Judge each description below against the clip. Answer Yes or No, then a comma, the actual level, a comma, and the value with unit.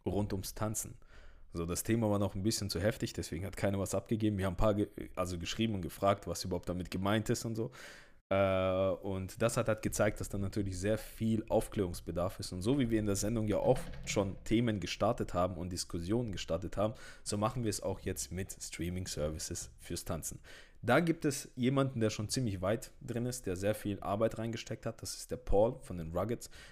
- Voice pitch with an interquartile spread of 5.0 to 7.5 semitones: No, average, 3.6 semitones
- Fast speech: Yes, fast, 215 wpm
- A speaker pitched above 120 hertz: No, low, 100 Hz